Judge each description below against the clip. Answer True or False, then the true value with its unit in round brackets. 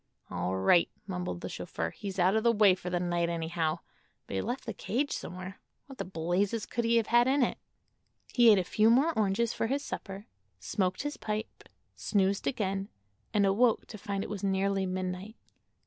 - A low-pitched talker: False (195 Hz)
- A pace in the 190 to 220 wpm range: True (195 wpm)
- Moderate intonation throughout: True (3.8 semitones)